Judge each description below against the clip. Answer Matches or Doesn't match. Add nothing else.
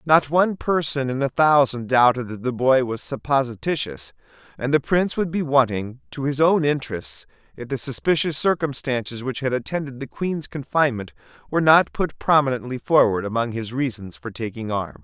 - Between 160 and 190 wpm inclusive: Matches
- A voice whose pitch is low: Matches